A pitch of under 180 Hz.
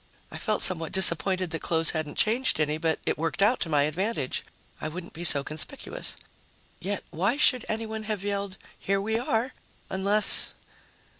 No: high, 190 Hz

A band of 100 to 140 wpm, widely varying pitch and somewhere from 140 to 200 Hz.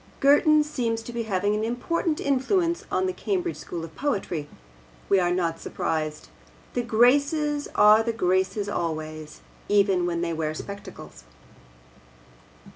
No: slow, 135 wpm; wide, 8.5 semitones; high, 210 Hz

